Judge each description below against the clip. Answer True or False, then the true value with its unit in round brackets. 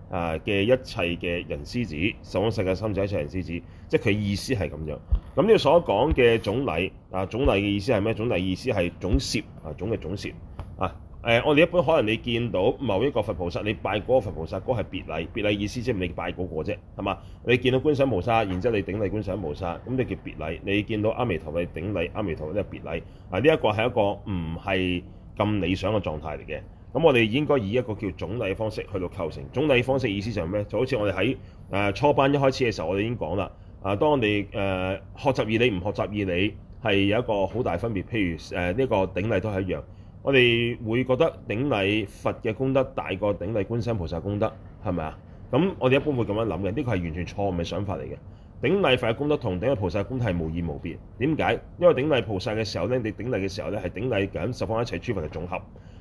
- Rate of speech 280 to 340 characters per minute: False (350 characters per minute)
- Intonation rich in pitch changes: False (4.3 semitones)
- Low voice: True (100 Hz)